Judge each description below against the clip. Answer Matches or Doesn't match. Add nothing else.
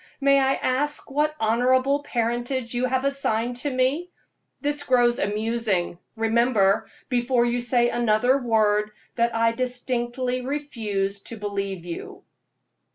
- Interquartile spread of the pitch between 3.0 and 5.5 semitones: Doesn't match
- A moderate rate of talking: Doesn't match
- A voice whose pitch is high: Matches